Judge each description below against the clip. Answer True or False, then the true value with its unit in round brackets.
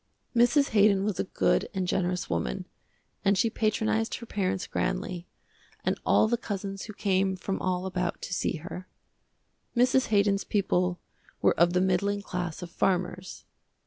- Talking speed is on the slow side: False (155 wpm)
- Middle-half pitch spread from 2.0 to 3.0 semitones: True (2.5 semitones)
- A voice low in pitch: False (190 Hz)